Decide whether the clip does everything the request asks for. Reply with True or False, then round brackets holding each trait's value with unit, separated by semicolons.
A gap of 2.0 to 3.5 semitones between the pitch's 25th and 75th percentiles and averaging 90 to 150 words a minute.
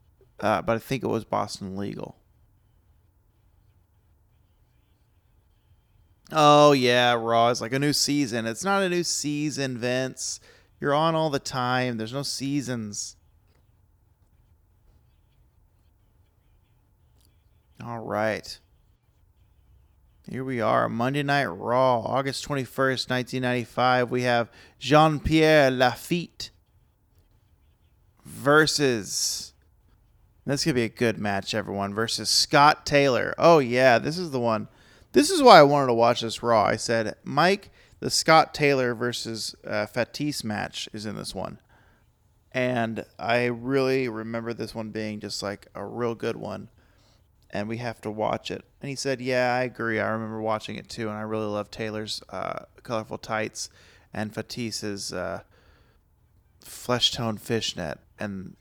False (4.0 semitones; 135 wpm)